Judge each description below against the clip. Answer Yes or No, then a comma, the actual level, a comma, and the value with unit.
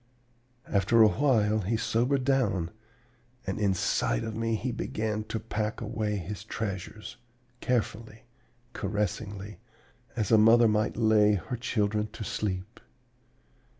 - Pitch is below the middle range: Yes, low, 110 Hz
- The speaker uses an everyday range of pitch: No, narrow, 1.8 semitones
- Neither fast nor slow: No, slow, 120 wpm